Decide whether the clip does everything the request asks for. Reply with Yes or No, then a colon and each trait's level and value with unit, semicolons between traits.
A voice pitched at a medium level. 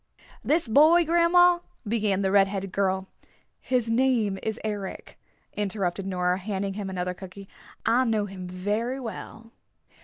No: high, 205 Hz